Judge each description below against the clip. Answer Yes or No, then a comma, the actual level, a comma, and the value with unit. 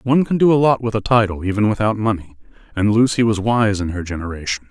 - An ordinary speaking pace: No, fast, 230 wpm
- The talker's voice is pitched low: Yes, low, 110 Hz